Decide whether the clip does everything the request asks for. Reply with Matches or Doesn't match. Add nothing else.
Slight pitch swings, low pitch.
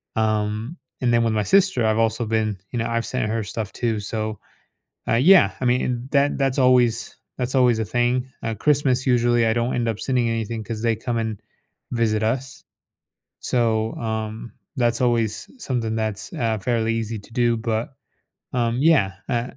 Matches